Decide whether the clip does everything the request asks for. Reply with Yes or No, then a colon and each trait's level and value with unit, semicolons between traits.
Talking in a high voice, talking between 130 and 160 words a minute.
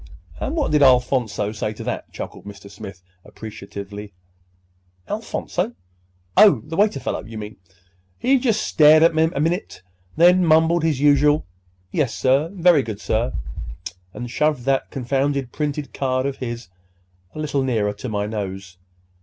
No: low, 135 Hz; average, 145 wpm